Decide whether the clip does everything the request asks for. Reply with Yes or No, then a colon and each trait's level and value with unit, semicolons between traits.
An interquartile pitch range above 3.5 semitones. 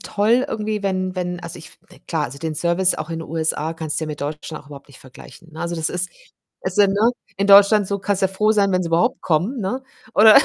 Yes: average, 4.0 semitones